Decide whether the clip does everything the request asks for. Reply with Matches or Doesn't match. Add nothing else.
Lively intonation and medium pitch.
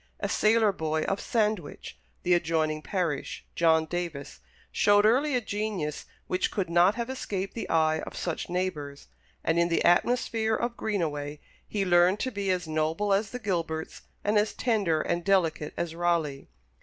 Doesn't match